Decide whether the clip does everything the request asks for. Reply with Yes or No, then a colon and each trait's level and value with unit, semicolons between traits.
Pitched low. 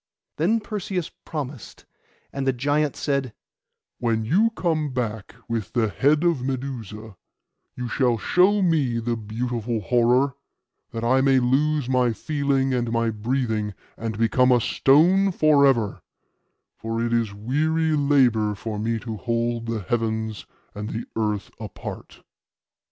Yes: low, 125 Hz